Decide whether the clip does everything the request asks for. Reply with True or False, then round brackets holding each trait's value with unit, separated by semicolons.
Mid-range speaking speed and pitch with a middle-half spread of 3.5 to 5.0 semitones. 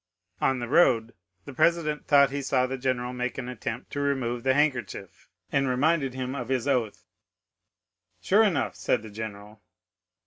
False (165 wpm; 2.7 semitones)